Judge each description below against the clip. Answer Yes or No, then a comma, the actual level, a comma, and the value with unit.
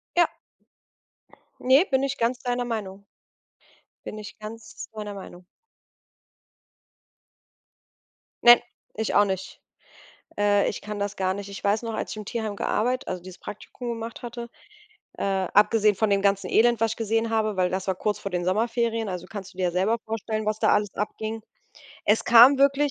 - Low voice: No, high, 215 Hz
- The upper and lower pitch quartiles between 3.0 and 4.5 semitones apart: No, narrow, 2.6 semitones